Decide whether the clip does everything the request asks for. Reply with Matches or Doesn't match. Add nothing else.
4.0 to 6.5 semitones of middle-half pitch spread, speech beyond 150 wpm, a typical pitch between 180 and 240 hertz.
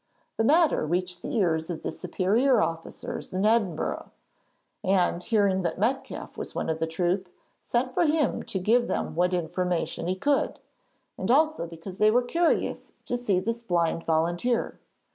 Matches